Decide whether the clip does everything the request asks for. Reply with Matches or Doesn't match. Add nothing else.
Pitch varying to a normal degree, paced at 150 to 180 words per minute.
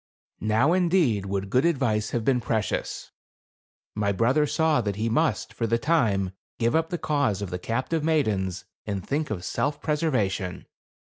Doesn't match